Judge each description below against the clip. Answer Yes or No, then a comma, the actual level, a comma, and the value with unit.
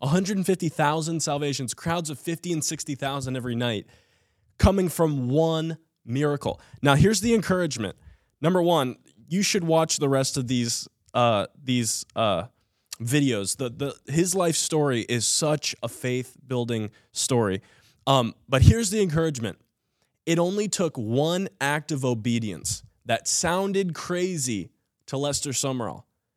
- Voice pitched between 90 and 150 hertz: Yes, medium, 140 Hz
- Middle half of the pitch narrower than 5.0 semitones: No, wide, 5.4 semitones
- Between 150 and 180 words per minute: No, slow, 135 wpm